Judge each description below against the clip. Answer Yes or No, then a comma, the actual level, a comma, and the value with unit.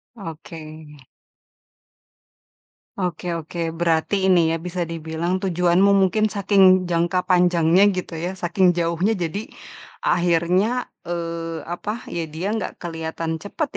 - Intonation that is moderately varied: No, narrow, 1.8 semitones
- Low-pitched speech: No, medium, 175 Hz